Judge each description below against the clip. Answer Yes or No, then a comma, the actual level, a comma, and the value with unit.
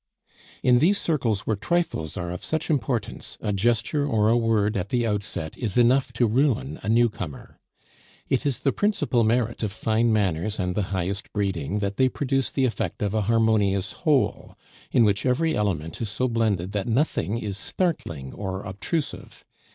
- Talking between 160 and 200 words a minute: Yes, average, 175 wpm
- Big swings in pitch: No, average, 4.2 semitones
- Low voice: Yes, low, 110 Hz